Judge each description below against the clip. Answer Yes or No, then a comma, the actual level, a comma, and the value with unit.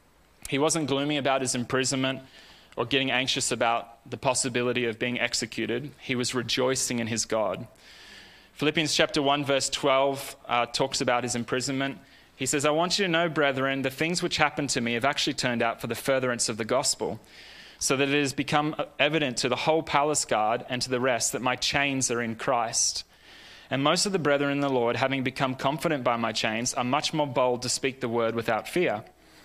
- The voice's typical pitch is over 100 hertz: Yes, low, 135 Hz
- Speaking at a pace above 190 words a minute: Yes, fast, 205 wpm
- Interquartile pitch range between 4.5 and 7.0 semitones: No, average, 2.8 semitones